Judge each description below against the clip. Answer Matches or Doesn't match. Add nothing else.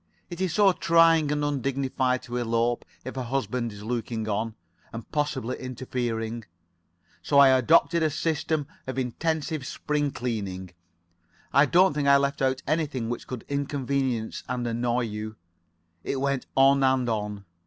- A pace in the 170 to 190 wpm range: Doesn't match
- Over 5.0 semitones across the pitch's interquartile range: Doesn't match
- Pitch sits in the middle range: Doesn't match